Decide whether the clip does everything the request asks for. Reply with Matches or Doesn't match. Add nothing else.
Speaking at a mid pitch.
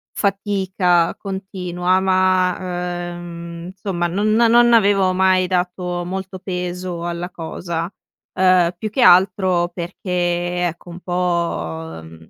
Matches